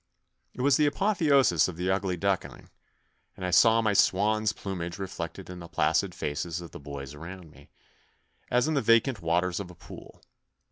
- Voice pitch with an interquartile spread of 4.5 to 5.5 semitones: Yes, average, 5.0 semitones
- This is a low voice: Yes, very low, 95 Hz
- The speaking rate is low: No, average, 180 wpm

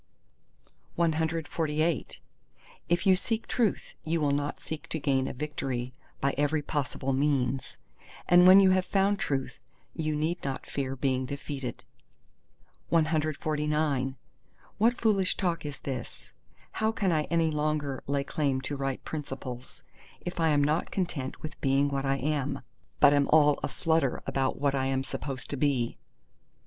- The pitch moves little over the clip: No, average, 3.1 semitones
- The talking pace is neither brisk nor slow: Yes, average, 150 wpm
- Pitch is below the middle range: No, medium, 150 Hz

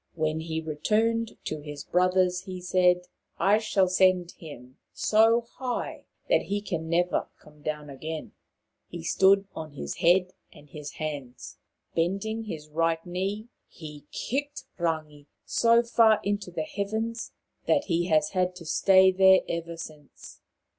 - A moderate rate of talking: Yes, average, 145 wpm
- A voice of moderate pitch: Yes, medium, 180 Hz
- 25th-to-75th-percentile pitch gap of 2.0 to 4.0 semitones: No, average, 4.4 semitones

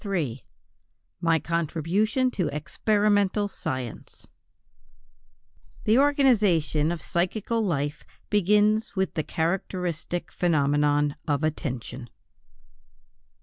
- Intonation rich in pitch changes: Yes, wide, 5.8 semitones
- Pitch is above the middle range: No, medium, 170 Hz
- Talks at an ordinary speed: No, slow, 80 wpm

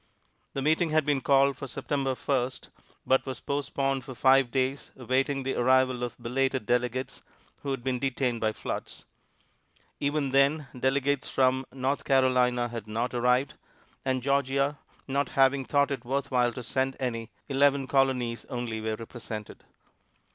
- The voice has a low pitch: Yes, low, 130 Hz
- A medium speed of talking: Yes, average, 150 wpm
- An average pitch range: No, narrow, 1.9 semitones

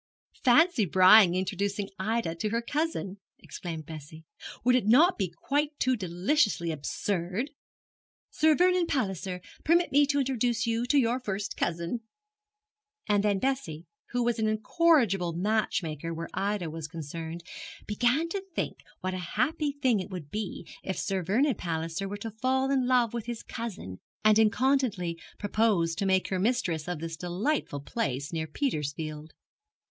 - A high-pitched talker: Yes, high, 205 Hz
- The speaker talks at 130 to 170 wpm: Yes, average, 150 wpm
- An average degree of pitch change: No, wide, 6.6 semitones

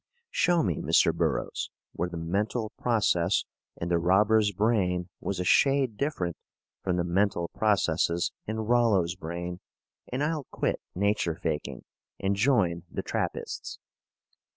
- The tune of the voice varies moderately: Yes, average, 4.2 semitones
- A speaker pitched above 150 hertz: No, very low, 95 Hz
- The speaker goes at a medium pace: No, slow, 130 wpm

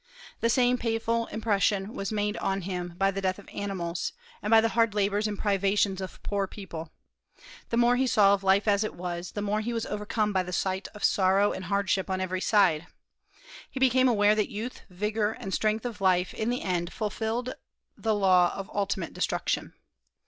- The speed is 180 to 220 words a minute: Yes, average, 195 wpm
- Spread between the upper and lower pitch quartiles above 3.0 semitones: No, narrow, 2.6 semitones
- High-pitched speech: Yes, high, 205 Hz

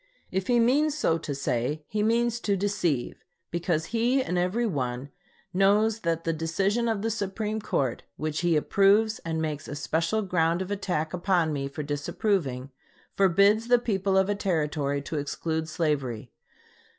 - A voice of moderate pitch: Yes, medium, 180 Hz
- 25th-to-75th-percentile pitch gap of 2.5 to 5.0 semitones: No, wide, 5.4 semitones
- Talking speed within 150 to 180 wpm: Yes, average, 160 wpm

